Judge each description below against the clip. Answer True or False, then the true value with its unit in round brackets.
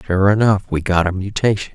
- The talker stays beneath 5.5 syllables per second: False (5.7 syllables/s)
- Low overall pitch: True (100 Hz)